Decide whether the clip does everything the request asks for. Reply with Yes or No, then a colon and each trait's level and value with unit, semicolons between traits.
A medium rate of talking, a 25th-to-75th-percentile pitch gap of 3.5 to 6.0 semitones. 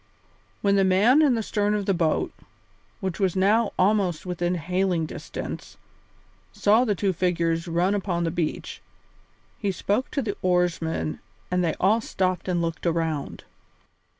No: average, 155 wpm; average, 3.1 semitones